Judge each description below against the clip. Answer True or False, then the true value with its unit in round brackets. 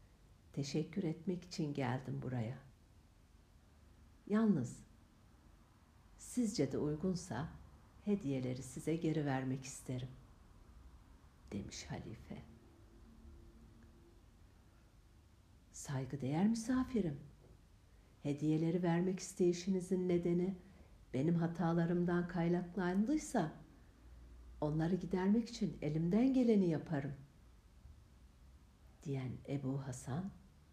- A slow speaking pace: True (70 wpm)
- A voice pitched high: False (135 Hz)